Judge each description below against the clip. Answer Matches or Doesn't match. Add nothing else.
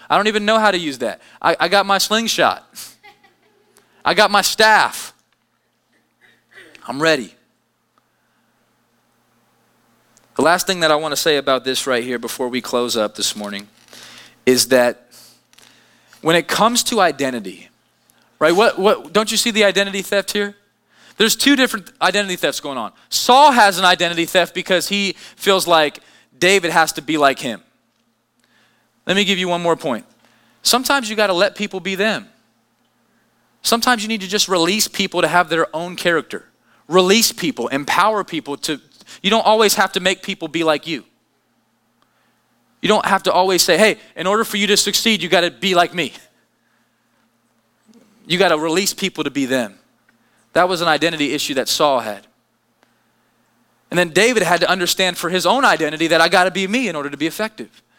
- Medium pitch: Matches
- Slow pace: Doesn't match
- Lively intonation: Matches